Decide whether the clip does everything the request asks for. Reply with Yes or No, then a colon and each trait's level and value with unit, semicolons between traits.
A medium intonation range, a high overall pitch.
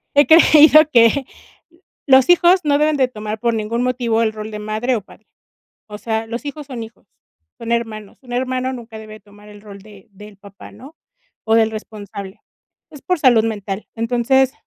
Yes: average, 3.4 semitones; high, 230 Hz